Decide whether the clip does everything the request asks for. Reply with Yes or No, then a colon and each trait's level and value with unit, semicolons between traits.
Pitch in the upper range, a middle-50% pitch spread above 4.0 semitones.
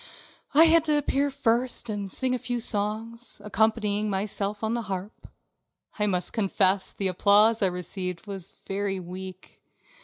No: high, 210 Hz; average, 3.3 semitones